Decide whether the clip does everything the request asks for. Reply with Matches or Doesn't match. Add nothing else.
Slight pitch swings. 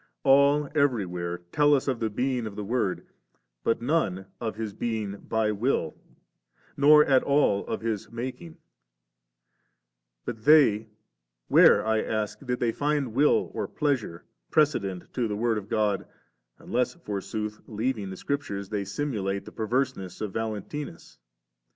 Doesn't match